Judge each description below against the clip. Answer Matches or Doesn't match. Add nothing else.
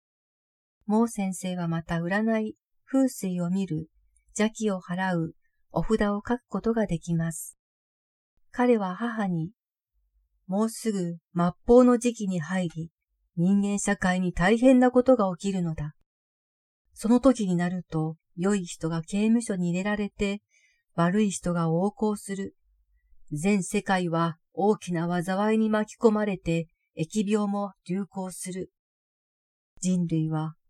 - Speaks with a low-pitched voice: Doesn't match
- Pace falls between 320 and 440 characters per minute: Doesn't match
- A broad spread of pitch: Doesn't match